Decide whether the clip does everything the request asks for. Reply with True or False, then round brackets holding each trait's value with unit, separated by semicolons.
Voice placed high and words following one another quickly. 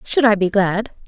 True (210 Hz; 220 wpm)